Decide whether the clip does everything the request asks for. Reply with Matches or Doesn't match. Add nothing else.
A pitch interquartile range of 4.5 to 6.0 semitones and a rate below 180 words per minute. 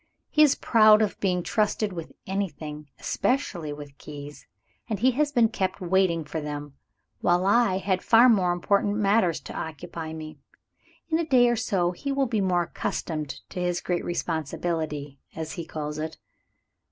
Matches